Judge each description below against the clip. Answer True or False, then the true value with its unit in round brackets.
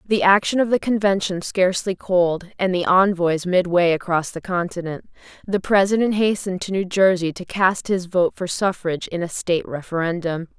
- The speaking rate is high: False (175 wpm)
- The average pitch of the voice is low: False (185 Hz)